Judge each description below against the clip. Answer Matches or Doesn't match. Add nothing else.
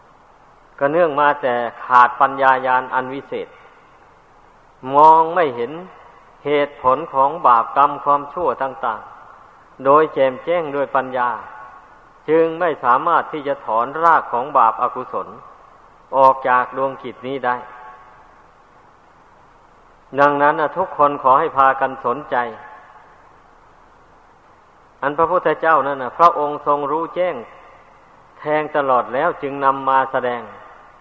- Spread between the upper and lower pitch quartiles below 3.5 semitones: Matches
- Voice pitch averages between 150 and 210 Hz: Doesn't match